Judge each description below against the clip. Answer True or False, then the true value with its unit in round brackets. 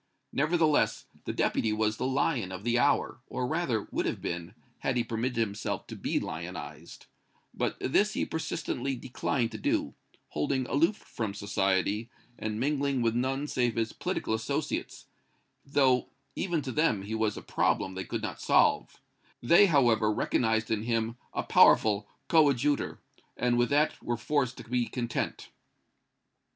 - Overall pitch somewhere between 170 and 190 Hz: False (120 Hz)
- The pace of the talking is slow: False (155 wpm)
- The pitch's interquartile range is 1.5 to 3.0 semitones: False (4.2 semitones)